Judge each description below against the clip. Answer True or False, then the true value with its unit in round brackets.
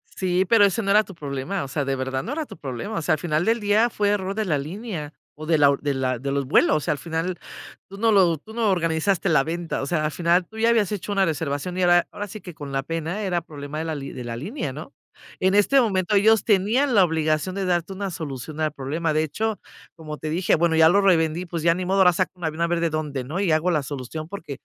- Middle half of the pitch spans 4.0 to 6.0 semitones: True (4.5 semitones)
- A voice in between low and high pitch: True (170 Hz)